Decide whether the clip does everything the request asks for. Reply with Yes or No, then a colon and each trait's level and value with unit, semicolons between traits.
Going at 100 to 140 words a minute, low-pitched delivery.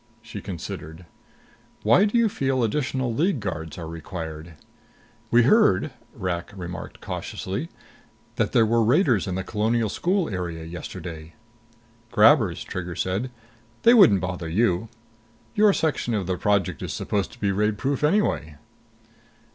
Yes: slow, 135 wpm; low, 105 Hz